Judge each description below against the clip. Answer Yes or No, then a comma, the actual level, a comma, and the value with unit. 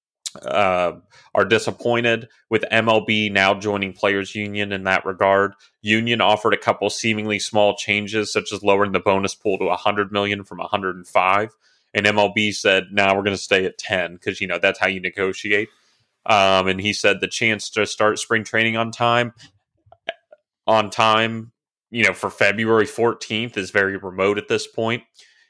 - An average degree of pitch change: No, narrow, 2.2 semitones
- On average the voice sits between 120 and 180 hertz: No, low, 105 Hz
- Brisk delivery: No, average, 170 wpm